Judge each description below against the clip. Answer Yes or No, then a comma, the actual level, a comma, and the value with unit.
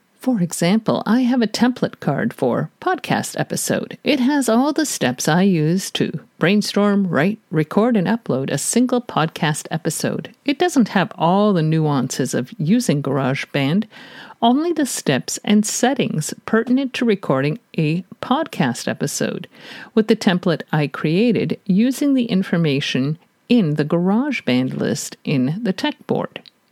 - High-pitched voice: Yes, high, 210 Hz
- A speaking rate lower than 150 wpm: Yes, average, 140 wpm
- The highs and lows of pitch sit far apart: Yes, wide, 7.2 semitones